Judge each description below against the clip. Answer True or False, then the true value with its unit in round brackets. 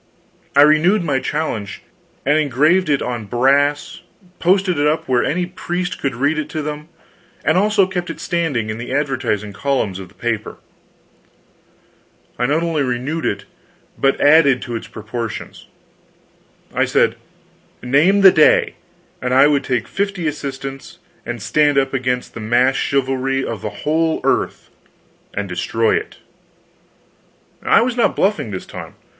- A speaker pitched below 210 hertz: True (140 Hz)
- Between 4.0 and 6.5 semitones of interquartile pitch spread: True (4.7 semitones)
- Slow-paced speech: False (150 wpm)